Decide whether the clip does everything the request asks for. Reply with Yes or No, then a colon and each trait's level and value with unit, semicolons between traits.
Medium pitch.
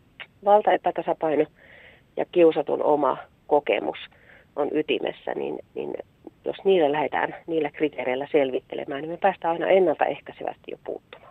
Yes: medium, 165 Hz